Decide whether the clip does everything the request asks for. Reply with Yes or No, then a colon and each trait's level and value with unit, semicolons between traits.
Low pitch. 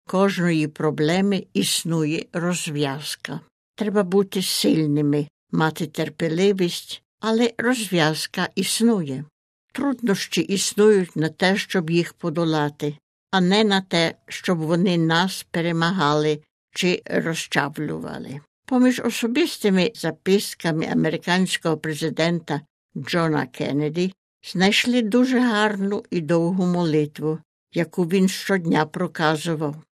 No: medium, 175 Hz